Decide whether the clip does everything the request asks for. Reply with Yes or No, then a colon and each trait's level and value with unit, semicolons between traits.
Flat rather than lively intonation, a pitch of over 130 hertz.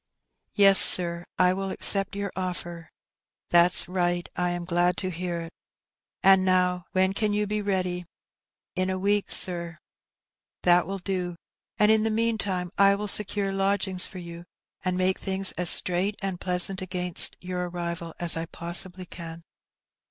Yes: narrow, 1.8 semitones; medium, 185 Hz